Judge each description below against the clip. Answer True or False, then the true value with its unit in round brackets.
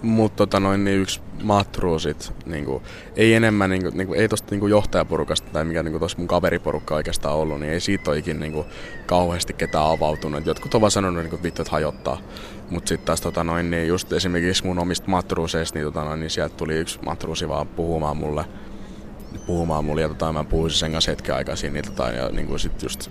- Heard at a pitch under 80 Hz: False (85 Hz)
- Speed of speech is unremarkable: False (195 wpm)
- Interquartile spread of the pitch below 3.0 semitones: False (3.4 semitones)